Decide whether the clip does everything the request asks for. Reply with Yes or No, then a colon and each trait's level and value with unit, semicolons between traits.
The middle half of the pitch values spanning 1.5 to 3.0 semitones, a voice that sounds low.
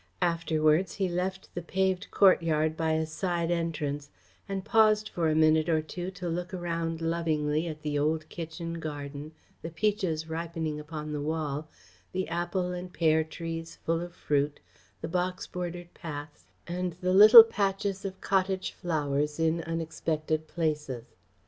No: narrow, 2.5 semitones; medium, 165 Hz